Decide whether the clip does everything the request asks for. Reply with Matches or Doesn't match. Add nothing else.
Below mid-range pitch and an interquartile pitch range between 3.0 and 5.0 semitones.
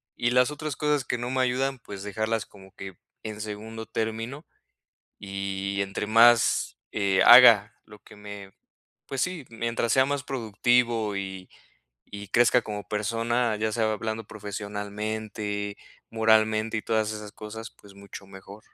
Doesn't match